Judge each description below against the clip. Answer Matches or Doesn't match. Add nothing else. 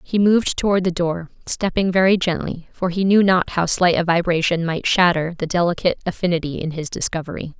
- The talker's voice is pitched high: Doesn't match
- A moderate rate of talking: Matches